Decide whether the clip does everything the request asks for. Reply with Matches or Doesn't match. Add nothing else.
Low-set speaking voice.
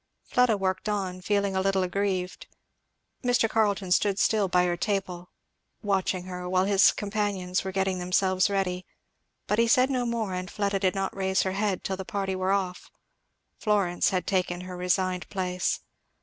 Doesn't match